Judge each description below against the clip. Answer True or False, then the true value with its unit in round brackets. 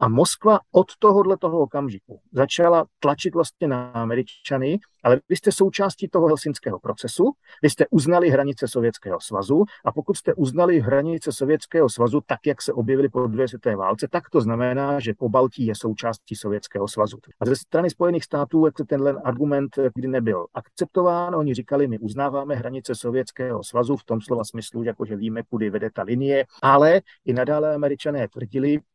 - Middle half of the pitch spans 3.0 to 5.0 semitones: True (4.3 semitones)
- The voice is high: False (140 Hz)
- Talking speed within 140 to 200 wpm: True (170 wpm)